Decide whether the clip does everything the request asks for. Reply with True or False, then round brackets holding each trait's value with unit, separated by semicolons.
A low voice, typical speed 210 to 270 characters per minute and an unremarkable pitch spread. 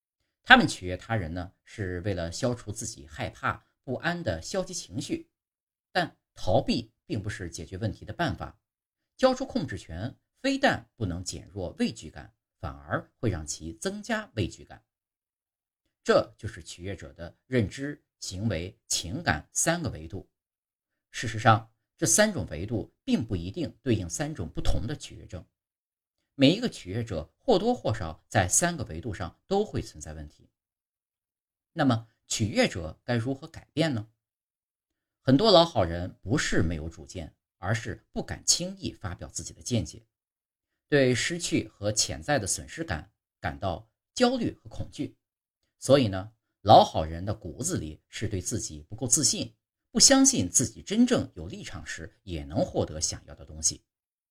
False (110 Hz; 235 characters per minute; 6.5 semitones)